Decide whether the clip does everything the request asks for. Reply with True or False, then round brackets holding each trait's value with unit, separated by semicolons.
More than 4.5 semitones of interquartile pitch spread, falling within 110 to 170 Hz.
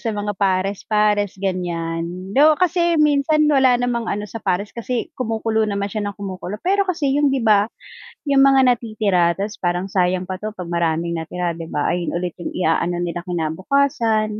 False (5.5 semitones; 205 Hz)